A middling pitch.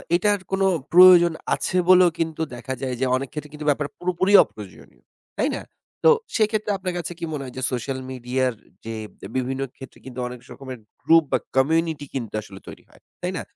Yes: medium, 150 Hz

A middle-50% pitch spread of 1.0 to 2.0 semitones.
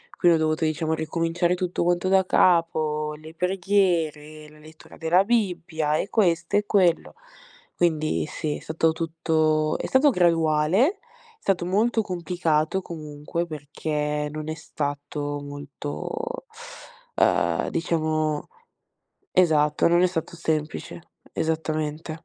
No: narrow, 2.4 semitones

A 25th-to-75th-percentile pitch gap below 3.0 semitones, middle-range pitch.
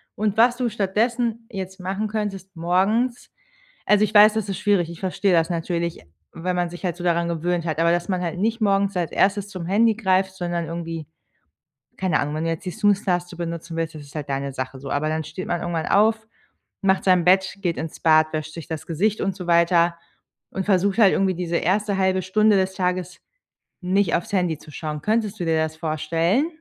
No: average, 3.3 semitones; medium, 180 Hz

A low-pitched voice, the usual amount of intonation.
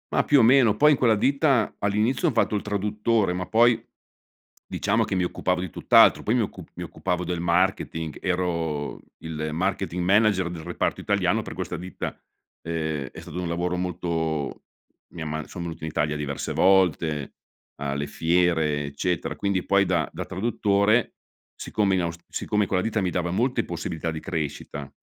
Yes: very low, 90 Hz; average, 4.2 semitones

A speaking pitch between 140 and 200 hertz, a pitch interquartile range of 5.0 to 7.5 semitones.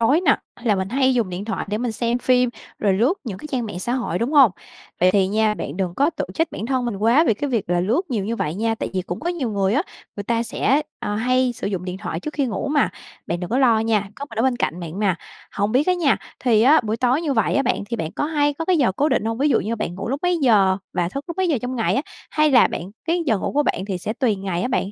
No: high, 230 Hz; wide, 5.6 semitones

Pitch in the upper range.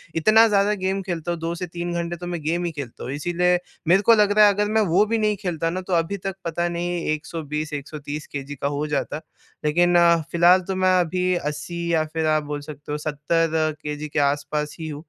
No: medium, 170 Hz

